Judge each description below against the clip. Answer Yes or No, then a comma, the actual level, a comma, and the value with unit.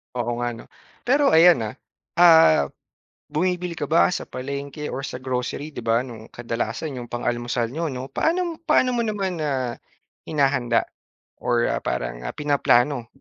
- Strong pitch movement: Yes, wide, 5.7 semitones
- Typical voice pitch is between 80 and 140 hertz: Yes, low, 135 Hz